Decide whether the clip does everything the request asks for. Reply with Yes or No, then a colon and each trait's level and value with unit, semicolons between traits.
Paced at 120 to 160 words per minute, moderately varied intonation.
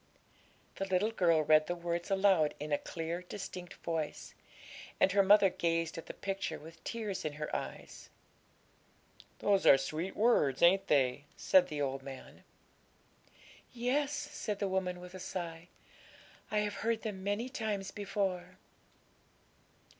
Yes: average, 145 wpm; average, 3.8 semitones